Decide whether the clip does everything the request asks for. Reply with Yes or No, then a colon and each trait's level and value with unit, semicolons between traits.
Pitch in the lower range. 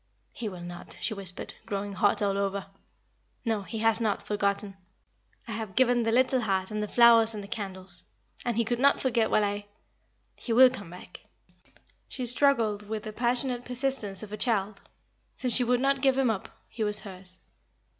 No: high, 215 Hz